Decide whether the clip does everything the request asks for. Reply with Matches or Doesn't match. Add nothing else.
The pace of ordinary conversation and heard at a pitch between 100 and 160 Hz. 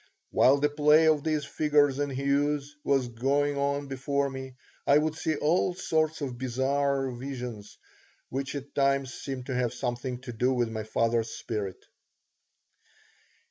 Matches